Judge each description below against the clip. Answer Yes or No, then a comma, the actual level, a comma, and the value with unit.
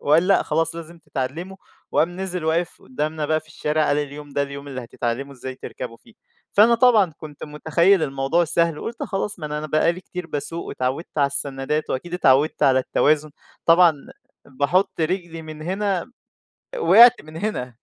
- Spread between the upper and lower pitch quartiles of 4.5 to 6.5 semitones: No, average, 3.7 semitones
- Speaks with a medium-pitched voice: Yes, medium, 155 Hz